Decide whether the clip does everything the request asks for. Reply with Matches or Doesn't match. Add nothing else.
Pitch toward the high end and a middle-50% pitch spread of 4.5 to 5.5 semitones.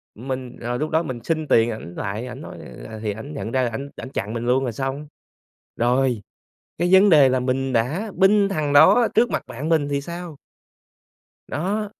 Doesn't match